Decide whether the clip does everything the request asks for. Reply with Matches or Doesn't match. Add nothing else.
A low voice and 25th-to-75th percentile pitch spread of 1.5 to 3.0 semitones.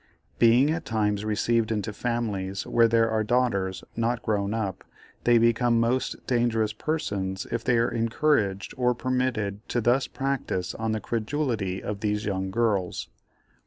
Matches